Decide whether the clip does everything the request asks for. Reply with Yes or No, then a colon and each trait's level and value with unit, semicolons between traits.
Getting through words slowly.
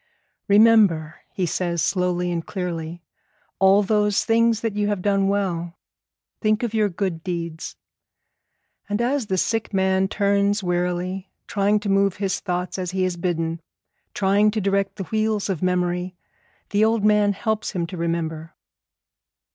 No: average, 150 wpm